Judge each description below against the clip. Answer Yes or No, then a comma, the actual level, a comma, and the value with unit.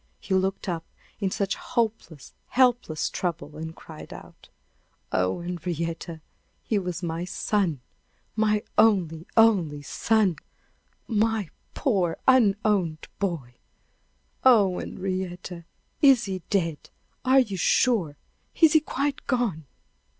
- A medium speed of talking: No, slow, 110 wpm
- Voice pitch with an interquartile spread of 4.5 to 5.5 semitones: Yes, average, 5.1 semitones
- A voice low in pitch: No, high, 190 Hz